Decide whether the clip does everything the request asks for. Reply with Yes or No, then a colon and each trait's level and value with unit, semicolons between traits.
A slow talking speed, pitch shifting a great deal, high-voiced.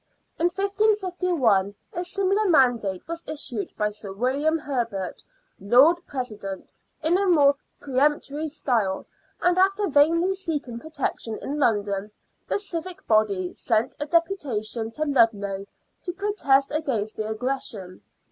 Yes: slow, 125 wpm; wide, 7.9 semitones; very high, 275 Hz